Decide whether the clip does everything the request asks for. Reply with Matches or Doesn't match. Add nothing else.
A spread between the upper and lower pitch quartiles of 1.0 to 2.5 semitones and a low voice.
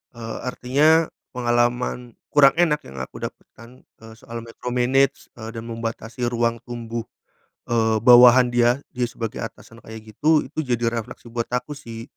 Matches